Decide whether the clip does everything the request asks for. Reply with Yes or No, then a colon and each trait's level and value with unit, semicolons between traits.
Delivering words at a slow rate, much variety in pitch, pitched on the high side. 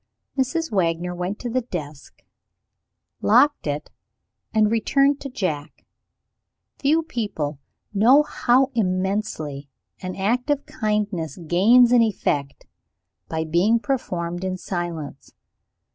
Yes: slow, 110 wpm; wide, 6.5 semitones; high, 200 Hz